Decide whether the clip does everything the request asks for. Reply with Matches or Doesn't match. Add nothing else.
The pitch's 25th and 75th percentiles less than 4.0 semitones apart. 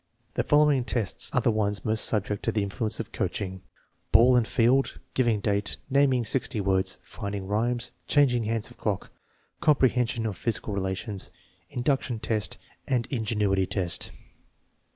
Matches